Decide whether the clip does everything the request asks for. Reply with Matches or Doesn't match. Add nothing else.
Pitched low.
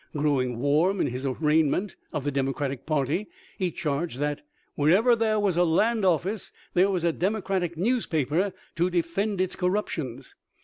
Doesn't match